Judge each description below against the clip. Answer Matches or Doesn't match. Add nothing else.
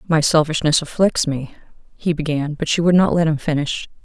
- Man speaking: Doesn't match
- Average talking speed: Matches